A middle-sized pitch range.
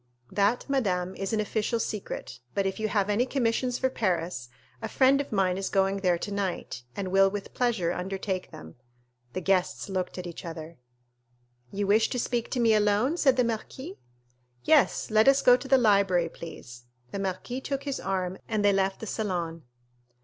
Yes: average, 4.1 semitones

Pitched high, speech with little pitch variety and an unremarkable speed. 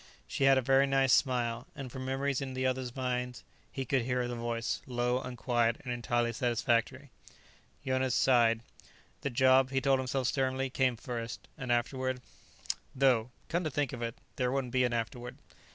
No: low, 125 Hz; narrow, 1.8 semitones; average, 180 wpm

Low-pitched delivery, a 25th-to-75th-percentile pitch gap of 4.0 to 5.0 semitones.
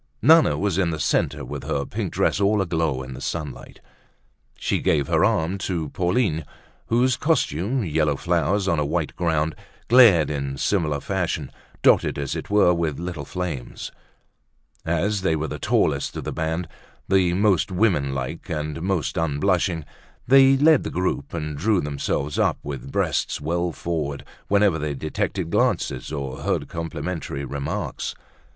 Yes: very low, 85 Hz; average, 4.5 semitones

